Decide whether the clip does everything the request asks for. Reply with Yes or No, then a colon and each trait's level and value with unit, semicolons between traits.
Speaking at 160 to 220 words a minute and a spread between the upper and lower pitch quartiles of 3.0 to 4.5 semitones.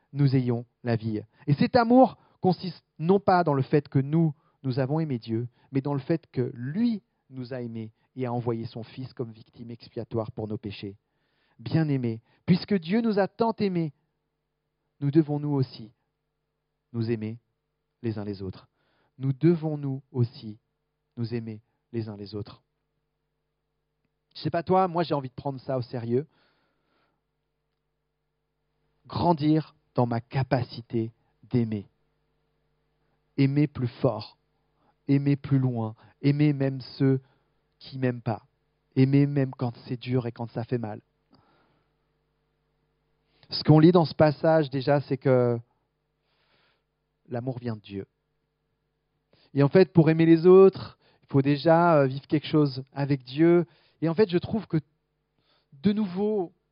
No: average, 150 wpm; average, 3.8 semitones